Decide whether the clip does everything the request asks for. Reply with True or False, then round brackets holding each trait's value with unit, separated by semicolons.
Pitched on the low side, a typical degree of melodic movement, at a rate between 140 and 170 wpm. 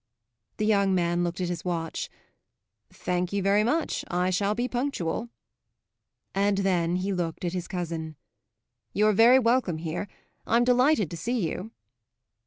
False (190 Hz; 4.1 semitones; 150 wpm)